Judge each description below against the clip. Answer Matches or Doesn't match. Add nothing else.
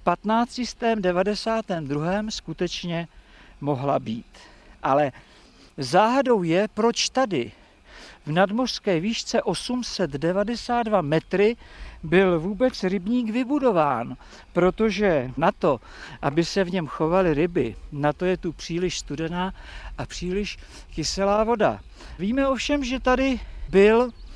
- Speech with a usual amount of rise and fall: Matches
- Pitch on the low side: Doesn't match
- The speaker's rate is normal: Doesn't match